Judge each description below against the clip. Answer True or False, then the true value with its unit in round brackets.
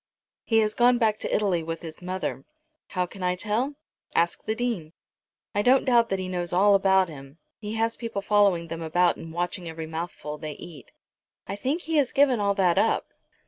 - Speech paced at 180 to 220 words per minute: True (200 wpm)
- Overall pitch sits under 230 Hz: True (190 Hz)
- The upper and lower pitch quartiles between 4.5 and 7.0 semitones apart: True (4.8 semitones)